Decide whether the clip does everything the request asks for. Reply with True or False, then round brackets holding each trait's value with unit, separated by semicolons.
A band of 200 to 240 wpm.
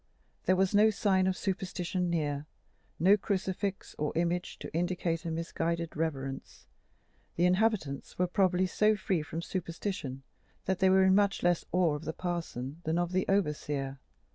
False (160 wpm)